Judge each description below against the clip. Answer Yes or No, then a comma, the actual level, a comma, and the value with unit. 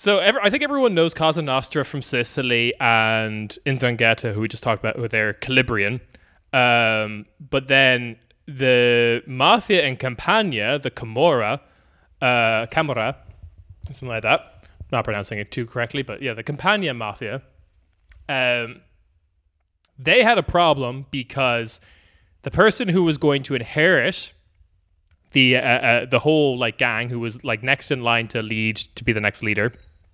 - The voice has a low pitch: Yes, low, 120 Hz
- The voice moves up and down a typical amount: Yes, average, 4.3 semitones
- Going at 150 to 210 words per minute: Yes, average, 155 wpm